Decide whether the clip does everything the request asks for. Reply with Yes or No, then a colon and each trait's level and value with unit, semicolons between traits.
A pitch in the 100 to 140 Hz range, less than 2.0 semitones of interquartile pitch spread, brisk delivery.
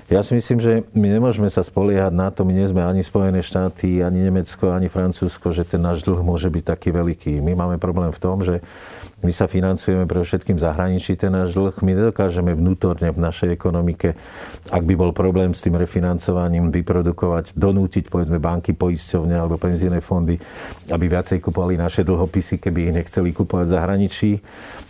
No: very low, 90 Hz; narrow, 1.5 semitones; fast, 180 wpm